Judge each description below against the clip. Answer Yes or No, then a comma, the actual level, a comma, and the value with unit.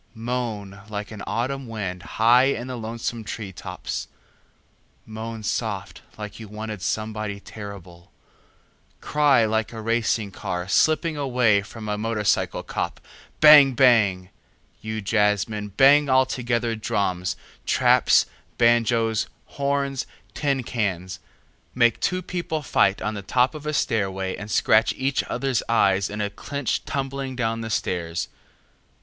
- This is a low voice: Yes, low, 110 Hz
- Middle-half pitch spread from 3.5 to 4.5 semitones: Yes, average, 3.8 semitones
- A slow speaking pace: Yes, slow, 130 wpm